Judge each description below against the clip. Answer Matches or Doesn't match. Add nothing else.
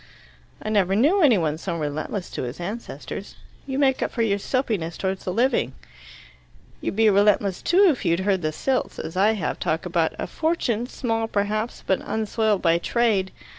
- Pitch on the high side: Matches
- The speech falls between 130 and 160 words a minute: Doesn't match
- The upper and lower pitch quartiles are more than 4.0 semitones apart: Matches